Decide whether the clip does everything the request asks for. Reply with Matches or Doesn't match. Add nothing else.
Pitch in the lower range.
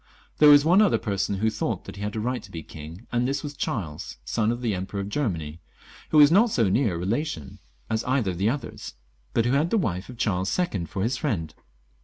Matches